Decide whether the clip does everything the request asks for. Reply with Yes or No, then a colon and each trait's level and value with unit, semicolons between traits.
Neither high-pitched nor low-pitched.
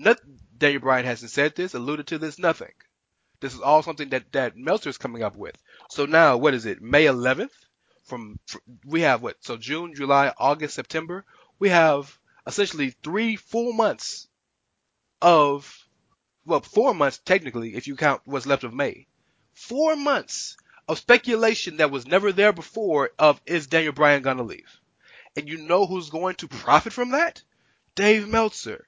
Yes: medium, 155 Hz